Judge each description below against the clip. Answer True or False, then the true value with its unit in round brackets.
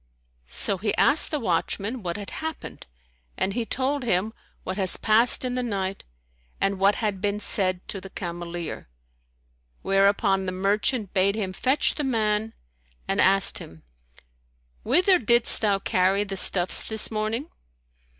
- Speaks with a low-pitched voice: False (200 Hz)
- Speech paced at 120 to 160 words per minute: True (150 wpm)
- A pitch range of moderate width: True (3.2 semitones)